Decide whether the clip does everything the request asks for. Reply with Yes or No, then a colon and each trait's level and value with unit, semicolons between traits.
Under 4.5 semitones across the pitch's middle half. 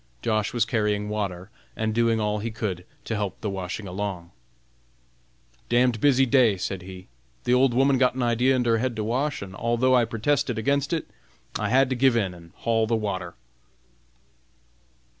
Yes: average, 3.5 semitones